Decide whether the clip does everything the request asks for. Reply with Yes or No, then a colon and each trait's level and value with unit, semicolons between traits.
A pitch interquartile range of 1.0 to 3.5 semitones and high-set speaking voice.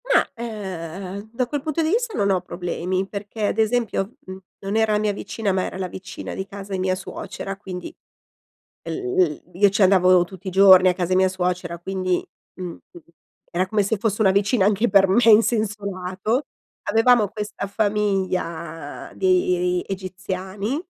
Yes: narrow, 2.5 semitones; high, 195 Hz